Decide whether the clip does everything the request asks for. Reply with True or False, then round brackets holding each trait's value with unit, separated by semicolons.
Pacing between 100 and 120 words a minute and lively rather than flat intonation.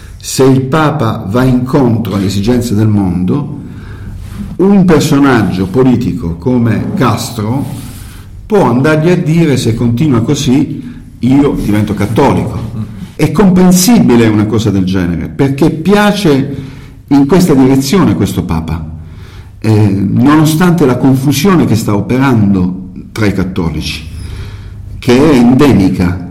True (115 wpm; 6.1 semitones)